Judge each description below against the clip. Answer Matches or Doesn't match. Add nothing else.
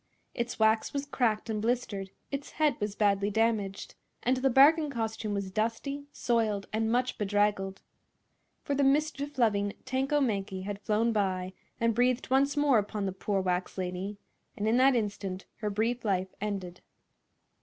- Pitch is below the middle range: Doesn't match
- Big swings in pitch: Doesn't match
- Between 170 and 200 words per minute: Doesn't match